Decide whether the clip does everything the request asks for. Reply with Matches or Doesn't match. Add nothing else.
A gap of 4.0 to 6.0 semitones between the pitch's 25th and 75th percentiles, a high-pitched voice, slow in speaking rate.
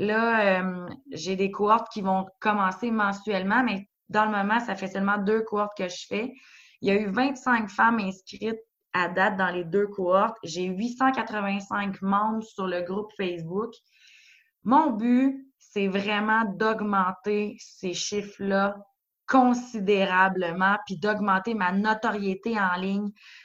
Doesn't match